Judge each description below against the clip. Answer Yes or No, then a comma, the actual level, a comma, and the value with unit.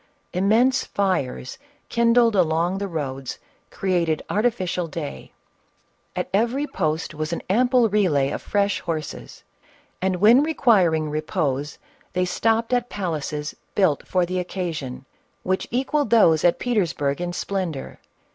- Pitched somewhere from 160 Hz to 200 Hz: Yes, medium, 185 Hz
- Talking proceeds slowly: Yes, slow, 125 wpm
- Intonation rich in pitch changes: Yes, wide, 6.0 semitones